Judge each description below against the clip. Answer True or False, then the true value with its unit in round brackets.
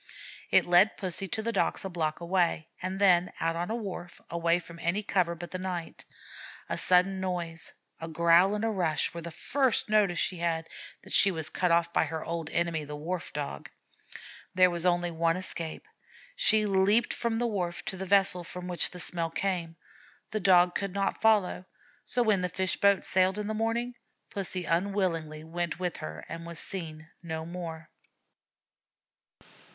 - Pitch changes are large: False (2.7 semitones)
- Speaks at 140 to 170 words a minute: False (180 wpm)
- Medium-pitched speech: True (180 Hz)